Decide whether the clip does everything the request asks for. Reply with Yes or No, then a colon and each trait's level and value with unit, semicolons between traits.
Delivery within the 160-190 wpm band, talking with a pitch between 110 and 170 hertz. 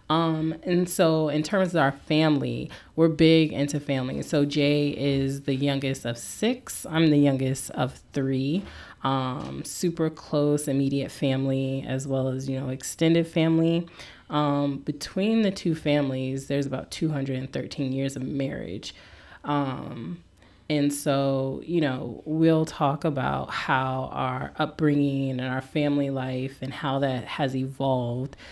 No: average, 140 wpm; medium, 140 Hz